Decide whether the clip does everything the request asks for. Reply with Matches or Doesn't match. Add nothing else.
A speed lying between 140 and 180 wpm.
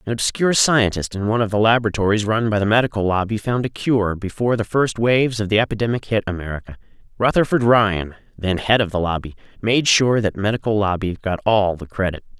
Doesn't match